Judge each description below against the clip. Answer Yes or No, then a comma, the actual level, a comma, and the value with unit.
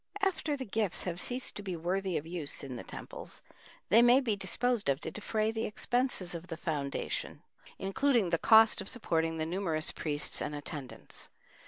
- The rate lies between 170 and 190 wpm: Yes, average, 180 wpm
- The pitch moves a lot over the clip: Yes, wide, 5.7 semitones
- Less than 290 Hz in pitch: Yes, high, 190 Hz